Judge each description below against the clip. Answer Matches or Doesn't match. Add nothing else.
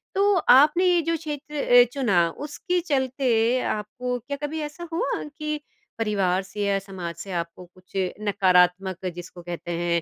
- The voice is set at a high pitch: Matches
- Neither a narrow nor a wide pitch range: Doesn't match